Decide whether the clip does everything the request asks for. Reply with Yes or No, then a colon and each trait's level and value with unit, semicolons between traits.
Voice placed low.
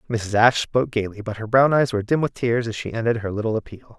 Yes: low, 115 Hz